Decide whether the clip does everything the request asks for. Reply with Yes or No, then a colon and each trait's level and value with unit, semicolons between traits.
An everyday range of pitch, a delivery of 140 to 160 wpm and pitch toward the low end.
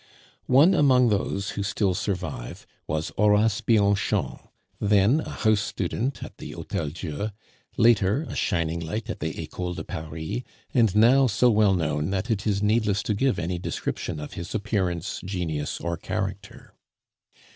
Yes: average, 4.5 semitones; average, 155 wpm; low, 100 Hz